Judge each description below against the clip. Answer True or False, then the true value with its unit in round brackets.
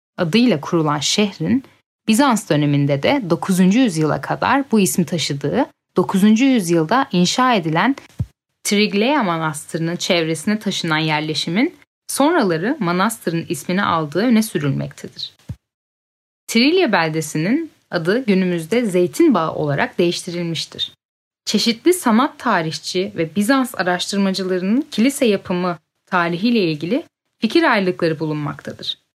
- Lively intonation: True (5.9 semitones)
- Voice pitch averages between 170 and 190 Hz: True (185 Hz)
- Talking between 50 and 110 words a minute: True (95 wpm)